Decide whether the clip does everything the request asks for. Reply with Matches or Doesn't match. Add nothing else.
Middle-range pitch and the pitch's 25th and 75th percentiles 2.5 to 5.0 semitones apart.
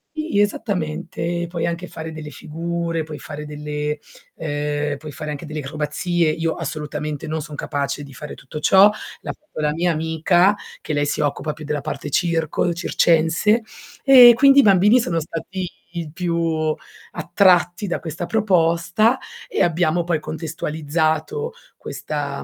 Matches